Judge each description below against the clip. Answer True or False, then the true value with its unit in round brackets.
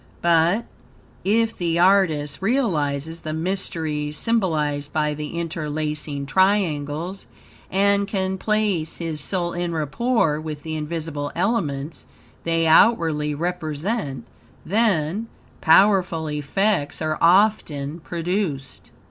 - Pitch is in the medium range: True (165 Hz)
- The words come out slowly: True (100 wpm)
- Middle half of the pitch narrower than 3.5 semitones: False (4.3 semitones)